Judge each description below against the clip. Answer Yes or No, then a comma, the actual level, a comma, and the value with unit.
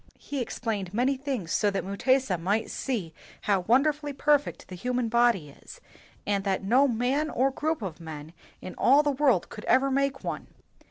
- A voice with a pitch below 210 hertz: No, high, 240 Hz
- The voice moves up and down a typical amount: No, wide, 5.9 semitones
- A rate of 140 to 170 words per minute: No, average, 185 wpm